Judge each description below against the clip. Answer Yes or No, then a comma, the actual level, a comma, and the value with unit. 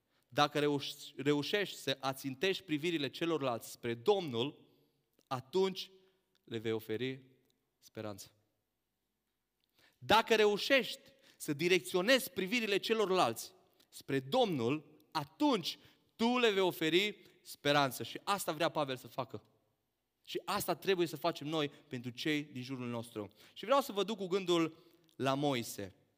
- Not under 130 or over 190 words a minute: No, average, 120 wpm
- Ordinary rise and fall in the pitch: No, wide, 6.7 semitones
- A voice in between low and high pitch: Yes, medium, 150 Hz